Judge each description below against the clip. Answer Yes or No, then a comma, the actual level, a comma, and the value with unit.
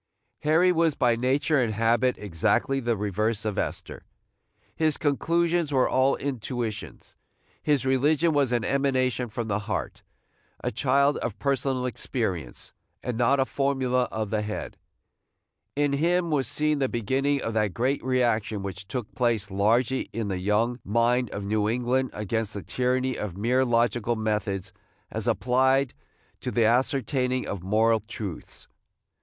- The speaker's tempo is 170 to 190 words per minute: No, average, 150 wpm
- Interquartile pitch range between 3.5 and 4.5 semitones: Yes, average, 3.9 semitones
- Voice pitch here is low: Yes, low, 125 Hz